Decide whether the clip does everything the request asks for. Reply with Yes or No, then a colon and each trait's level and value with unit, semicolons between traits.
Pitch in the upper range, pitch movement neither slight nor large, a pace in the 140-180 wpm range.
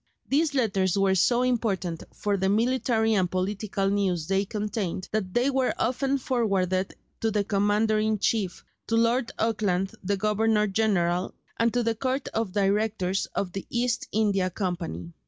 Yes: high, 210 Hz; average, 3.1 semitones; average, 155 wpm